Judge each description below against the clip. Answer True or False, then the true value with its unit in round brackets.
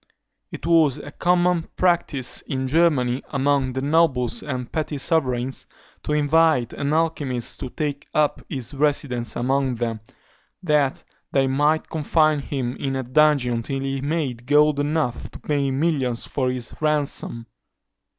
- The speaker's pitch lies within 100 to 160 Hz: True (140 Hz)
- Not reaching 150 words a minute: True (140 wpm)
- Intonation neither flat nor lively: True (3.0 semitones)